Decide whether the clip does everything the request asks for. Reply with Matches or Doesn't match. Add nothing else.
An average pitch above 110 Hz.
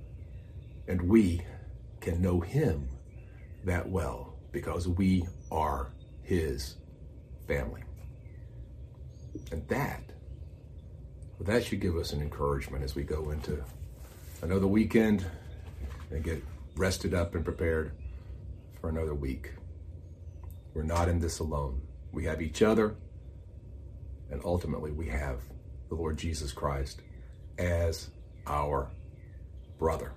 Doesn't match